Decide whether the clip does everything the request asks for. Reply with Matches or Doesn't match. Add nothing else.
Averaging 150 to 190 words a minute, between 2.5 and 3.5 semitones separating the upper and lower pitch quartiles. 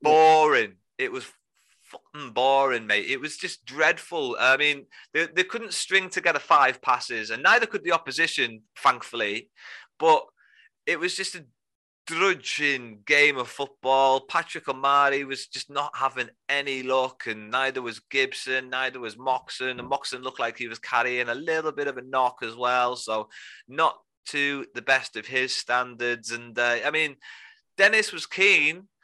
Doesn't match